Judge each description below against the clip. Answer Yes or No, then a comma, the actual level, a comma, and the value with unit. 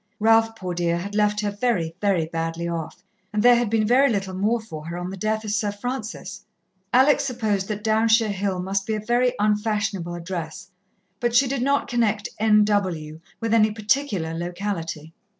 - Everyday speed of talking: Yes, average, 180 wpm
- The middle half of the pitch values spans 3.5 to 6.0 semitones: Yes, average, 3.9 semitones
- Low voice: No, high, 210 Hz